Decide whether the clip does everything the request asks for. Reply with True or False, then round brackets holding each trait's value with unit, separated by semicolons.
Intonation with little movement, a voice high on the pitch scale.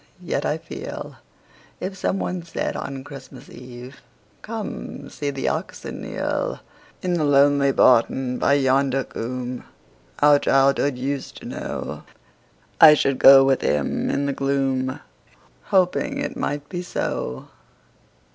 False (2.0 semitones; 140 Hz)